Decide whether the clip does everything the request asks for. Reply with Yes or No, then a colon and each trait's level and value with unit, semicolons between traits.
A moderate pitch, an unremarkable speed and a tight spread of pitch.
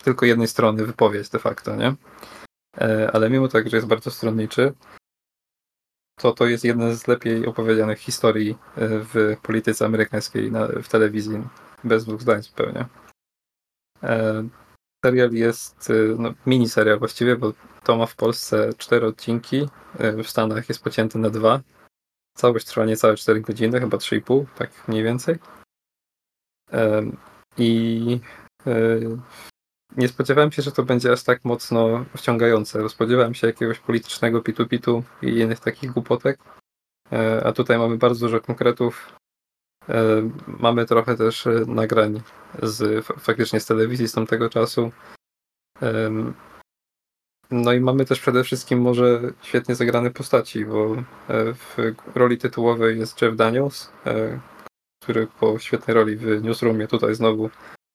No: low, 115 Hz; average, 125 wpm; narrow, 1.7 semitones